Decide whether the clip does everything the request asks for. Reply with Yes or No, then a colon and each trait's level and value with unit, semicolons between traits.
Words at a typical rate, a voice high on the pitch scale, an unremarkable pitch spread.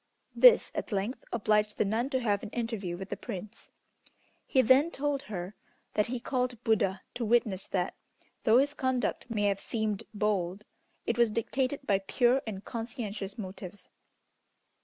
Yes: average, 160 wpm; high, 220 Hz; average, 3.9 semitones